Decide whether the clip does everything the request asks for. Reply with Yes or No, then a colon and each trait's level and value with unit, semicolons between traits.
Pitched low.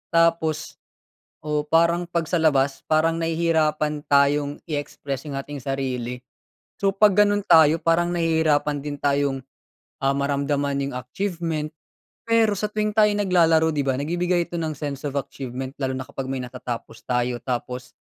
No: medium, 150 Hz